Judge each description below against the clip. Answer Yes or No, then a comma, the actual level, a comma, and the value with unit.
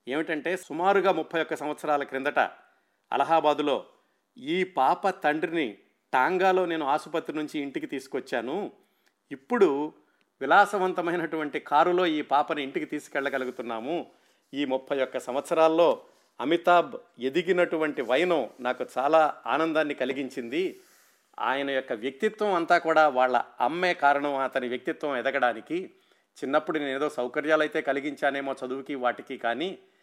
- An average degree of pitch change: Yes, average, 4.3 semitones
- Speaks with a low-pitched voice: No, medium, 155 Hz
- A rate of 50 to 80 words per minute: No, average, 110 wpm